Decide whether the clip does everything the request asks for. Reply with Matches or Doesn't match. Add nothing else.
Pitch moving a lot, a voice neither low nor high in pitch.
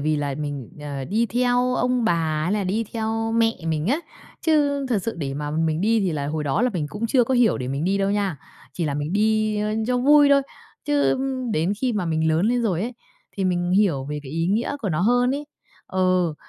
Doesn't match